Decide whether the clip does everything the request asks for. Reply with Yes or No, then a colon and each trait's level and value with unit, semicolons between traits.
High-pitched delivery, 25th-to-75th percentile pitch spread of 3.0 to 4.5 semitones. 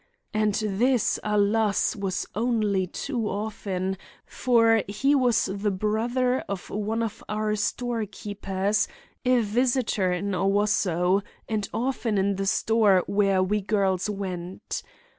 No: high, 210 Hz; narrow, 2.5 semitones